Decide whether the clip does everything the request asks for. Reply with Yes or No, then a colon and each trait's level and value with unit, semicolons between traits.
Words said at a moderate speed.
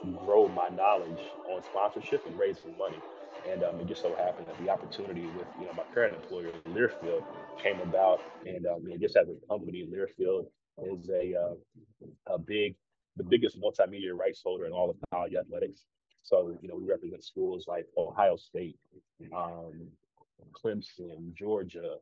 Yes: average, 165 wpm